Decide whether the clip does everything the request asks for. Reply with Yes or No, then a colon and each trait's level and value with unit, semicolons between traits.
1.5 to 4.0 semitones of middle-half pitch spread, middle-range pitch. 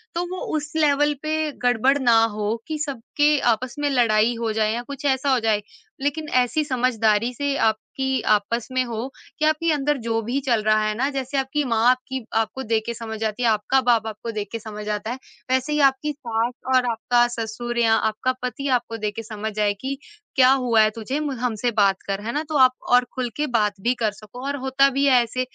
No: average, 3.6 semitones; high, 245 Hz